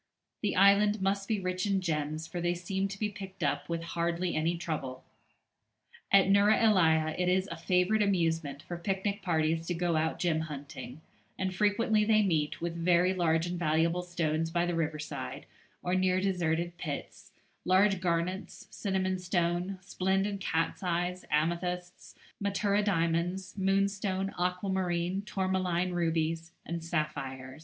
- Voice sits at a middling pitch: Yes, medium, 180 Hz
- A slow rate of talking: No, average, 145 wpm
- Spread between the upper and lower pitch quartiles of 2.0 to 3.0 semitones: Yes, narrow, 2.6 semitones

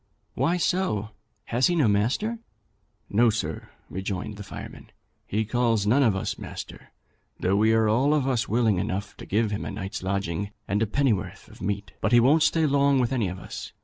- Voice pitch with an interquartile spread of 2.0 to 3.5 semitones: No, average, 4.7 semitones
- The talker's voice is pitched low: Yes, low, 110 Hz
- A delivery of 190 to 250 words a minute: Yes, average, 195 wpm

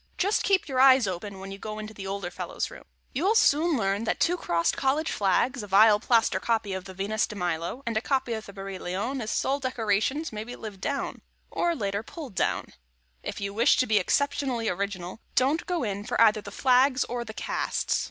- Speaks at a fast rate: Yes, fast, 210 wpm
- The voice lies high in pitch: Yes, high, 220 Hz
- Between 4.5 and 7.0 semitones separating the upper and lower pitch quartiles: Yes, average, 5.0 semitones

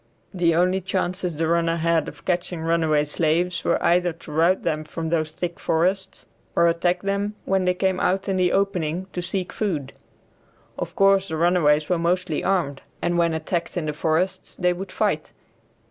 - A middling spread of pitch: No, narrow, 2.3 semitones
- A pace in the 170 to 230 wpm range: Yes, average, 180 wpm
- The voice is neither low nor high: Yes, medium, 175 Hz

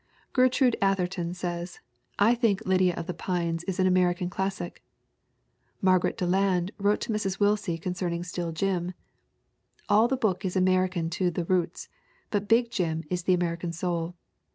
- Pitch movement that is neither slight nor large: No, narrow, 2.1 semitones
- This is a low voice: No, medium, 185 Hz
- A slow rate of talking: No, average, 155 wpm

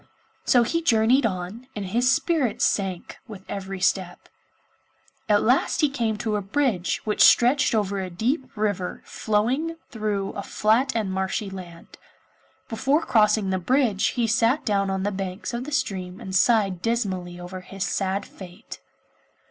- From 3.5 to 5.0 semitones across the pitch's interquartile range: Yes, average, 4.1 semitones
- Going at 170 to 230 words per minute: No, average, 155 wpm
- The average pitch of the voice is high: Yes, high, 210 Hz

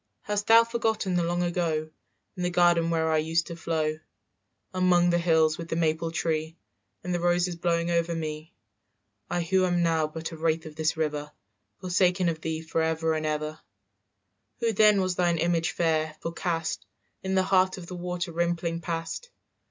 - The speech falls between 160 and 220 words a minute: Yes, average, 175 wpm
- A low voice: No, medium, 170 Hz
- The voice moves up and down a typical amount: No, narrow, 1.8 semitones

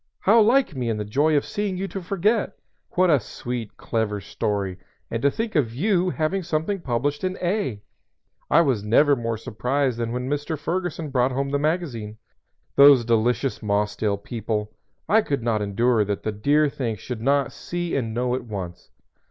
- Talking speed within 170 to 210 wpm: Yes, average, 185 wpm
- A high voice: No, low, 130 Hz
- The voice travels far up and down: Yes, wide, 6.6 semitones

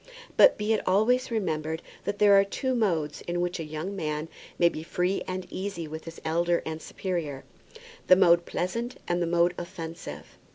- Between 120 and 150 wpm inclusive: No, average, 180 wpm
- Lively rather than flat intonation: No, average, 3.5 semitones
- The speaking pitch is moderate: Yes, medium, 175 Hz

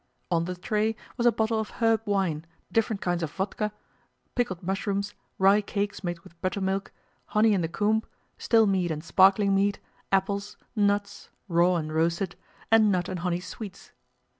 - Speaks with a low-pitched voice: No, high, 195 Hz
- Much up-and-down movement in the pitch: No, average, 2.9 semitones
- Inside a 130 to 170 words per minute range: Yes, average, 165 wpm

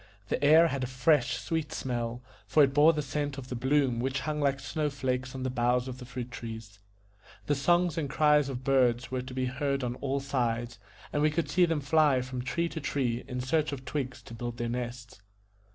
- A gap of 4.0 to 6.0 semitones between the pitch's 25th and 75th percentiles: No, average, 2.9 semitones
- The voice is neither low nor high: No, low, 130 Hz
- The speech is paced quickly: Yes, fast, 225 wpm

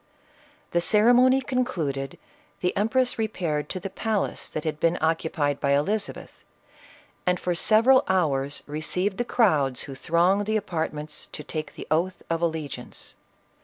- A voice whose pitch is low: No, medium, 170 Hz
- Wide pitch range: Yes, wide, 5.9 semitones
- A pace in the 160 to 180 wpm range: No, average, 150 wpm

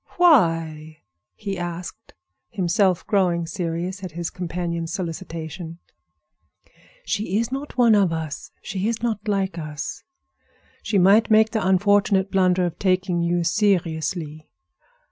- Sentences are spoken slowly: Yes, slow, 125 wpm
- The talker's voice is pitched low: No, medium, 185 Hz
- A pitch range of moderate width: Yes, average, 3.4 semitones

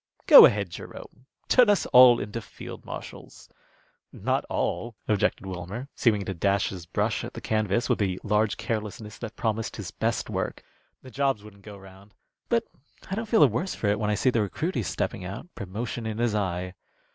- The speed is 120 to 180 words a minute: No, average, 190 wpm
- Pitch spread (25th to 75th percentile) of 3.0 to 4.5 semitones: Yes, average, 3.3 semitones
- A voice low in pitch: Yes, low, 105 Hz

